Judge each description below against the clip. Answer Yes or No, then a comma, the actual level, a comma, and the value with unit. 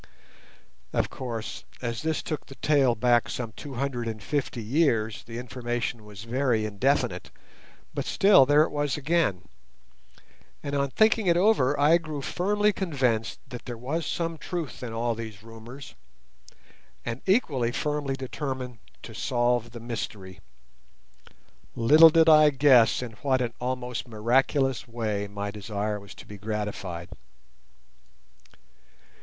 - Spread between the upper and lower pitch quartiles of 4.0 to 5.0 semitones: Yes, average, 4.5 semitones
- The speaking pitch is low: Yes, low, 125 Hz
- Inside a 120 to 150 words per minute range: Yes, average, 140 wpm